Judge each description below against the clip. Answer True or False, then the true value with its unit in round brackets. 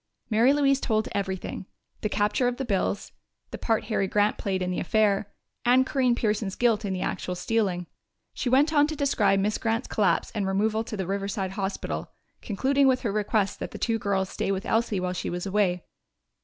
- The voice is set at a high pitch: True (210 Hz)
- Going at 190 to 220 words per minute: True (195 wpm)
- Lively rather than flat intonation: False (3.5 semitones)